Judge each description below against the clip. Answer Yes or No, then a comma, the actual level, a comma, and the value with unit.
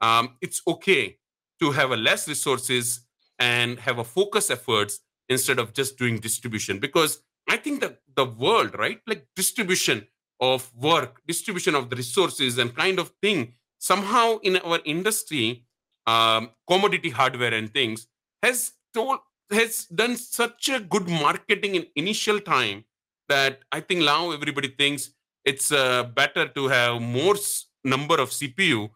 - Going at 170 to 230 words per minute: No, average, 150 wpm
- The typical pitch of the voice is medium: Yes, medium, 145 Hz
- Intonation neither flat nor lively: No, wide, 7.8 semitones